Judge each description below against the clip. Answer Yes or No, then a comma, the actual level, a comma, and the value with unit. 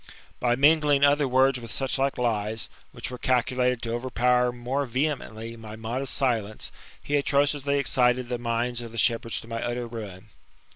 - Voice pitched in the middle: No, low, 125 Hz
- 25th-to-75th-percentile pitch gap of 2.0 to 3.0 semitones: Yes, narrow, 2.6 semitones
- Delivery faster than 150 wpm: Yes, average, 165 wpm